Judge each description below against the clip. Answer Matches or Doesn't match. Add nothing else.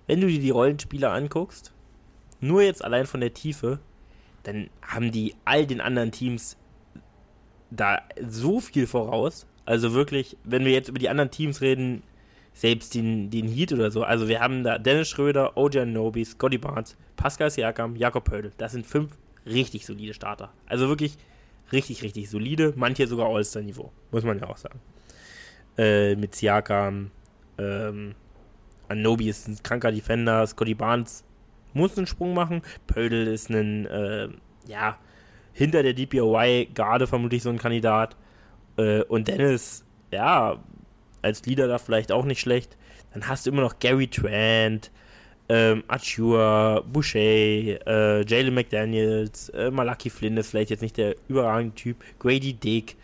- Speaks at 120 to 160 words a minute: Matches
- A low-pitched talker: Matches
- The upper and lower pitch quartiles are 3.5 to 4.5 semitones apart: Doesn't match